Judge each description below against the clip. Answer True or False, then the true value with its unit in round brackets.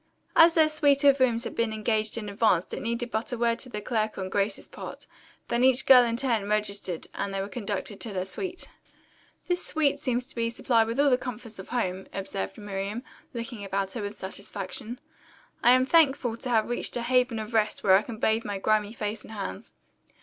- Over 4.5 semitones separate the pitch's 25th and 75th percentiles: False (3.5 semitones)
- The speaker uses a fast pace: True (215 wpm)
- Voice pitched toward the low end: False (225 Hz)